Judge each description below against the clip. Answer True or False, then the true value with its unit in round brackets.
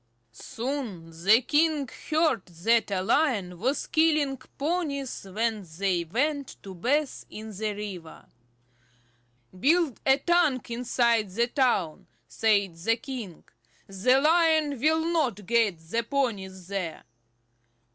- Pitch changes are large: True (6.7 semitones)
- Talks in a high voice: True (235 Hz)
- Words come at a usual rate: False (120 wpm)